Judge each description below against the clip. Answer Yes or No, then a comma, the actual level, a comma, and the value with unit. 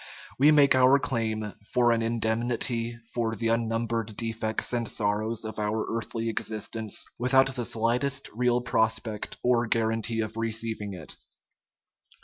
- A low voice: Yes, low, 115 Hz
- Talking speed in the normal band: No, slow, 130 wpm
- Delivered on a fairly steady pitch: Yes, narrow, 1.4 semitones